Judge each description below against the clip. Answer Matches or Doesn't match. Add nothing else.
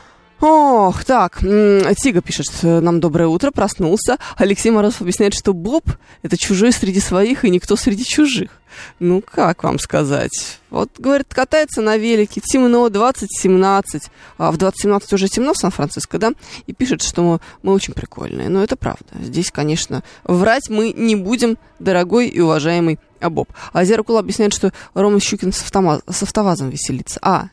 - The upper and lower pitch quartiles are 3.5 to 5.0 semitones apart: Matches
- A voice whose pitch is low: Doesn't match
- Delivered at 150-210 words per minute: Matches